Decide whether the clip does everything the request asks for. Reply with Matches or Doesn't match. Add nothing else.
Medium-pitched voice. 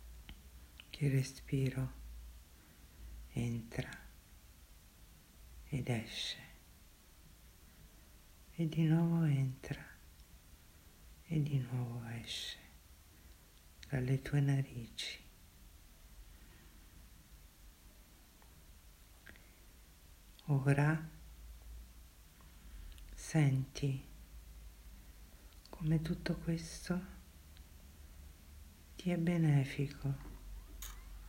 Doesn't match